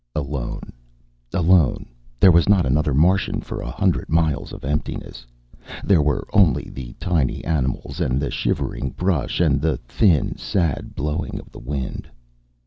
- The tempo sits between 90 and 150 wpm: Yes, average, 145 wpm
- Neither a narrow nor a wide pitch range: Yes, average, 4.3 semitones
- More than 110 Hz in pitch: No, very low, 75 Hz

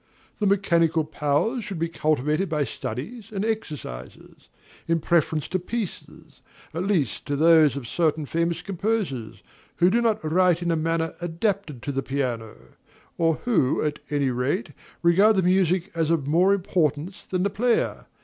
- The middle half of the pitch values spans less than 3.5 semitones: No, average, 4.5 semitones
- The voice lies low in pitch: No, medium, 165 Hz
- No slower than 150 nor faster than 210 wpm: Yes, average, 160 wpm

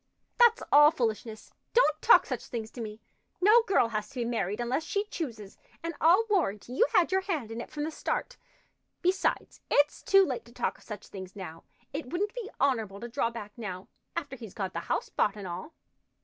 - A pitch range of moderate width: No, wide, 8.0 semitones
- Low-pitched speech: No, high, 245 Hz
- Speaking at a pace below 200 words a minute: No, fast, 205 wpm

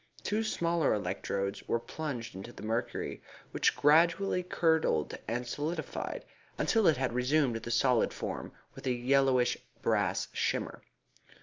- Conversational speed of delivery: No, slow, 130 wpm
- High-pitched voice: No, low, 130 Hz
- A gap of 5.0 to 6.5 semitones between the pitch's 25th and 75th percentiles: Yes, wide, 5.4 semitones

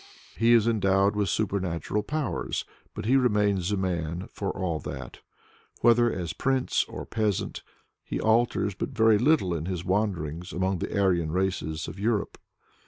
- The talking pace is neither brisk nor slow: Yes, average, 155 wpm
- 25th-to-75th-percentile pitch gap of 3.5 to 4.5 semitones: Yes, average, 3.9 semitones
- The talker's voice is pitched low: Yes, low, 100 Hz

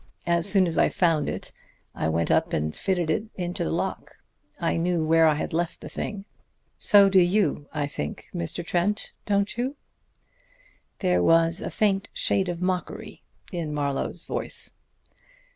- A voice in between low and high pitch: Yes, medium, 175 Hz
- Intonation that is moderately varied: Yes, average, 3.6 semitones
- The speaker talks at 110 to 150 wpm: No, average, 160 wpm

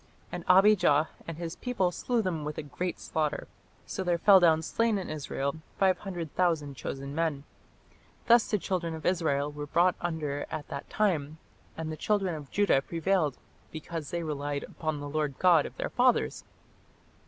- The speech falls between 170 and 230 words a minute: Yes, average, 175 wpm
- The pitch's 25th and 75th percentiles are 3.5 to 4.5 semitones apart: Yes, average, 3.8 semitones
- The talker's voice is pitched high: No, medium, 165 Hz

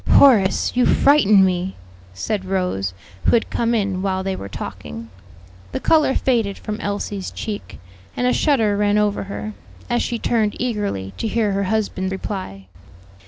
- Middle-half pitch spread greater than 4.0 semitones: No, average, 3.1 semitones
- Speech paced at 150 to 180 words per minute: Yes, average, 160 wpm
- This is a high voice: Yes, high, 205 Hz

